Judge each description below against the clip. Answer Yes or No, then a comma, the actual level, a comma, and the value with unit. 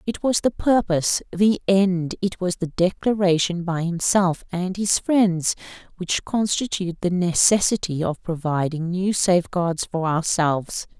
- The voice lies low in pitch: No, medium, 180 Hz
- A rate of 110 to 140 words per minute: Yes, slow, 135 wpm